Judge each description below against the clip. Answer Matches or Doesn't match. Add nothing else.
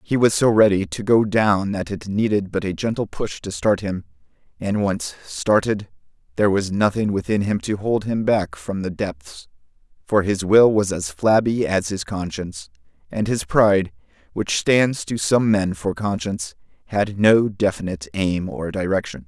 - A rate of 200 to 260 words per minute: Doesn't match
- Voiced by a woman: Doesn't match